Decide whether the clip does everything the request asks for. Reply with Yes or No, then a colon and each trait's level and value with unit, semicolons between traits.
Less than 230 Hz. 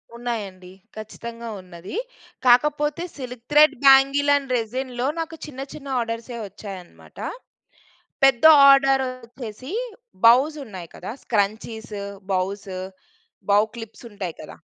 No: high, 235 Hz